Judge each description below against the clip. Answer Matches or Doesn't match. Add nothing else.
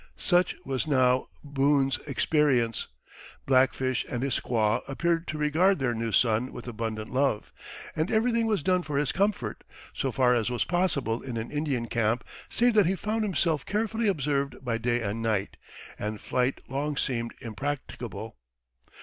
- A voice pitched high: Doesn't match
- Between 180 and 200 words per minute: Doesn't match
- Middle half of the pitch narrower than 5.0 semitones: Doesn't match